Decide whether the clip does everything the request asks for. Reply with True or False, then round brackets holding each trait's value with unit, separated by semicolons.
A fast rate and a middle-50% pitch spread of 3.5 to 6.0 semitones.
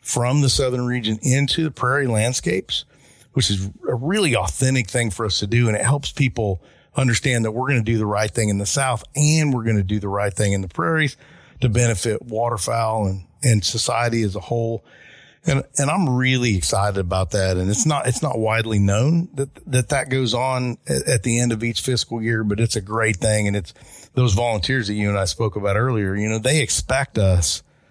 True (215 wpm; 3.8 semitones)